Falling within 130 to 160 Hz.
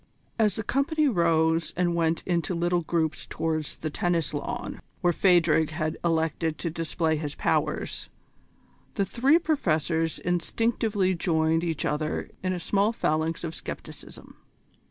No: medium, 170 Hz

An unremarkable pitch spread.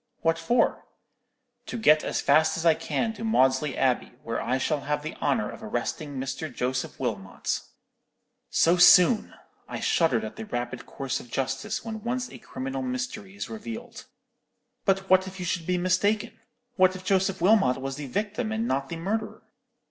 No: wide, 8.1 semitones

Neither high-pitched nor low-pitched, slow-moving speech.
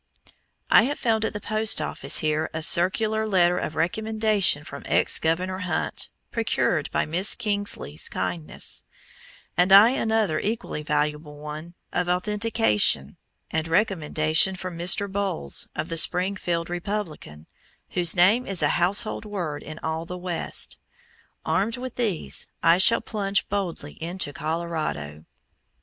Yes: medium, 180 Hz; slow, 130 wpm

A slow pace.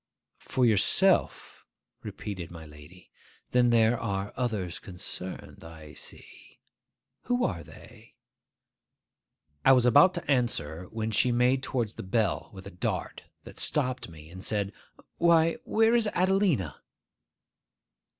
Yes: slow, 125 wpm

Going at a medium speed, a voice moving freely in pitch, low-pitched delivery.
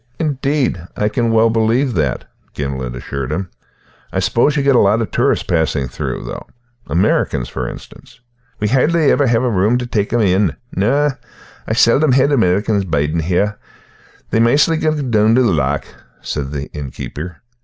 Yes: average, 170 wpm; wide, 7.3 semitones; low, 110 Hz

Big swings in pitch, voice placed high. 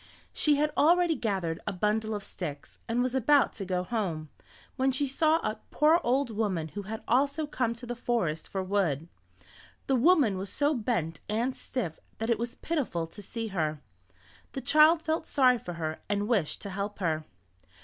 Yes: wide, 6.3 semitones; high, 225 Hz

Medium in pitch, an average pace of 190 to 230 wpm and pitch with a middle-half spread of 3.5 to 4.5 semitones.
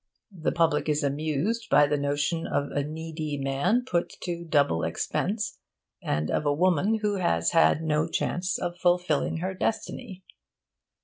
No: medium, 160 Hz; average, 150 wpm; average, 3.9 semitones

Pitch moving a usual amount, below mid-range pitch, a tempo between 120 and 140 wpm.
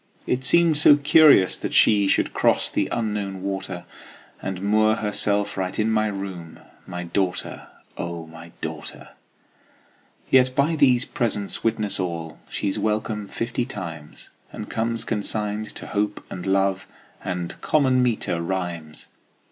Yes: average, 3.8 semitones; low, 105 Hz; slow, 135 wpm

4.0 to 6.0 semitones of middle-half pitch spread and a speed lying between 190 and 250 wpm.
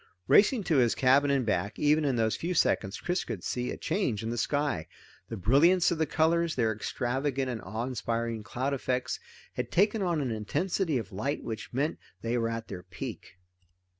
Yes: wide, 5.4 semitones; average, 195 wpm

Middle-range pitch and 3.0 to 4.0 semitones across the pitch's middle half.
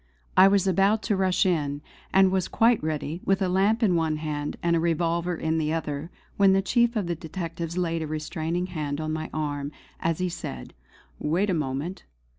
Yes: medium, 170 Hz; average, 3.4 semitones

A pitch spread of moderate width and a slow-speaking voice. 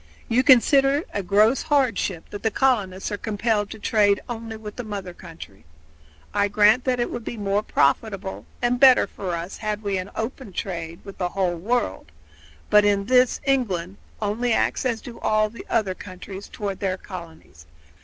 No: average, 3.6 semitones; average, 175 wpm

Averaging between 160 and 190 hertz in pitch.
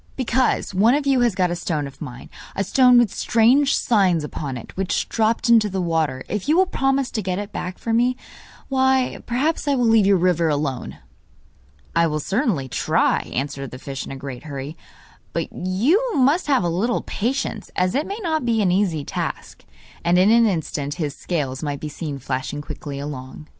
Yes: medium, 185 Hz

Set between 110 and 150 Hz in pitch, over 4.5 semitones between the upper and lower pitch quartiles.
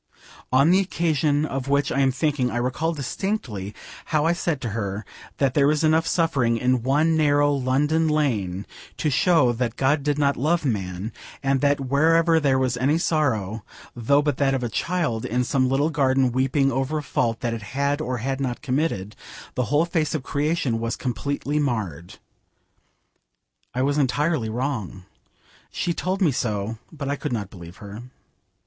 No: low, 135 Hz; average, 4.0 semitones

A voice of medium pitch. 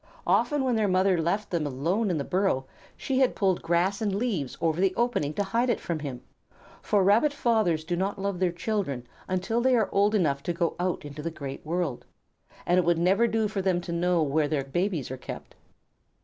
Yes: medium, 180 Hz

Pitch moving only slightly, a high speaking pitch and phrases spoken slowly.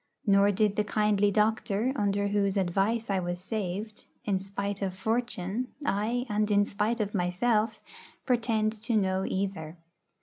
No: narrow, 1.9 semitones; high, 205 Hz; average, 145 wpm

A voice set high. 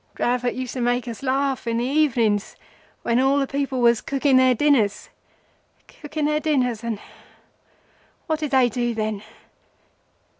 Yes: very high, 255 Hz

